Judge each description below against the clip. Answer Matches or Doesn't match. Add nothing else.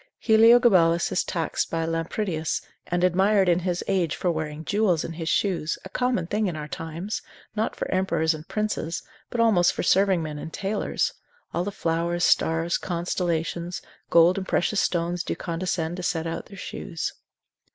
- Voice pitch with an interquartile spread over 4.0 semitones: Doesn't match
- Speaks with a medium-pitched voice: Matches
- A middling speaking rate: Matches